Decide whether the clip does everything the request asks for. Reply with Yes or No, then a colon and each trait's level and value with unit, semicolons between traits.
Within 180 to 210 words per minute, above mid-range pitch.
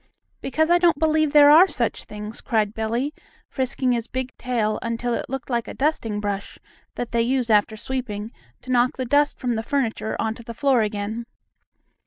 Yes: average, 185 wpm; high, 240 Hz